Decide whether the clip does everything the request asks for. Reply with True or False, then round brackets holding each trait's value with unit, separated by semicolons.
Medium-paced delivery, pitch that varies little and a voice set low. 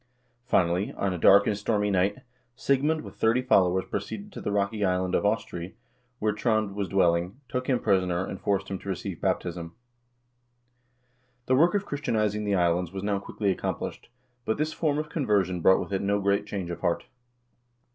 False (185 wpm; 3.3 semitones; 100 Hz)